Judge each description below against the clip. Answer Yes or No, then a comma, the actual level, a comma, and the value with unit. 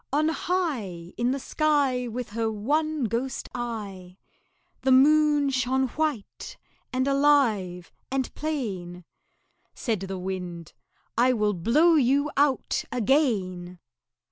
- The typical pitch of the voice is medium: No, very high, 250 Hz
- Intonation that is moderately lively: No, wide, 6.4 semitones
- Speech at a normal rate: No, slow, 115 wpm